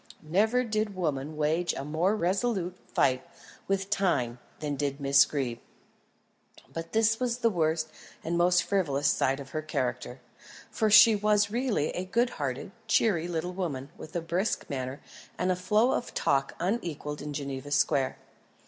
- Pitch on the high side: No, medium, 170 Hz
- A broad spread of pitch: Yes, wide, 6.1 semitones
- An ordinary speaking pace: Yes, average, 155 wpm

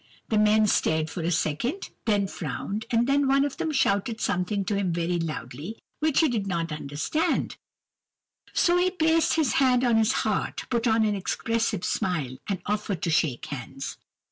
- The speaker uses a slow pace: No, average, 175 wpm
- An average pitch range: No, wide, 6.7 semitones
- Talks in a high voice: Yes, high, 210 Hz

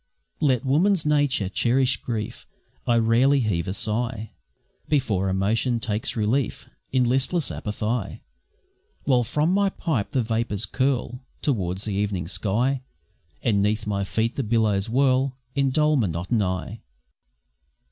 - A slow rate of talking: Yes, slow, 125 wpm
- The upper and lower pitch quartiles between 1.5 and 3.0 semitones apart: No, average, 4.4 semitones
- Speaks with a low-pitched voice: Yes, low, 115 Hz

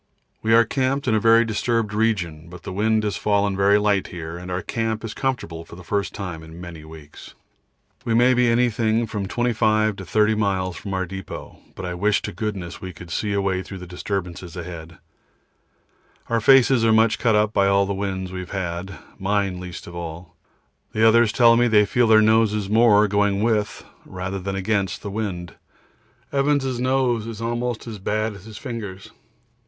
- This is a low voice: Yes, low, 105 Hz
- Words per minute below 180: No, average, 190 wpm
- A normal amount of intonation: Yes, average, 3.4 semitones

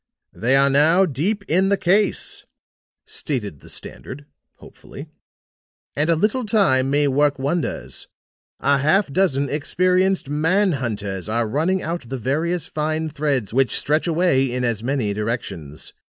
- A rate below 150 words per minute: Yes, average, 140 wpm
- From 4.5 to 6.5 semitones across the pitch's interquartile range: Yes, average, 5.1 semitones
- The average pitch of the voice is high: No, medium, 145 Hz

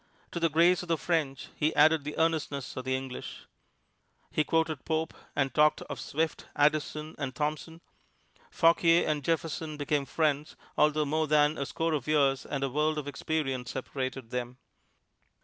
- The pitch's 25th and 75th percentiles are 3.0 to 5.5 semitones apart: No, narrow, 2.5 semitones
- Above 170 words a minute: No, average, 165 wpm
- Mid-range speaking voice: Yes, medium, 150 Hz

